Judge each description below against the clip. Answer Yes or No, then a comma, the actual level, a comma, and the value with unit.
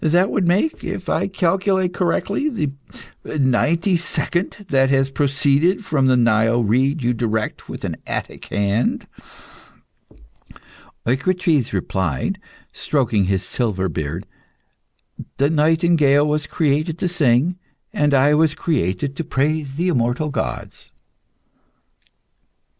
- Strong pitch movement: Yes, wide, 5.7 semitones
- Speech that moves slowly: Yes, slow, 115 wpm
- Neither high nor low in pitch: Yes, medium, 145 Hz